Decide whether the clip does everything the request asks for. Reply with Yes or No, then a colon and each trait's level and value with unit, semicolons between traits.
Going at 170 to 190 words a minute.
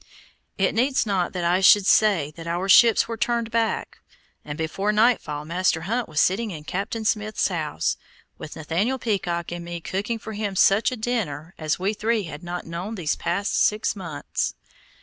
Yes: average, 175 wpm